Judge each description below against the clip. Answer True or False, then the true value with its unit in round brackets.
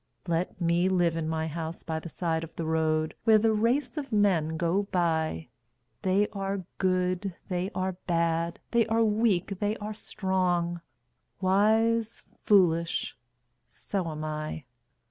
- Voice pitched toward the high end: False (180 Hz)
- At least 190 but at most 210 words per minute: False (145 wpm)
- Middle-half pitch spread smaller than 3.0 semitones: False (3.8 semitones)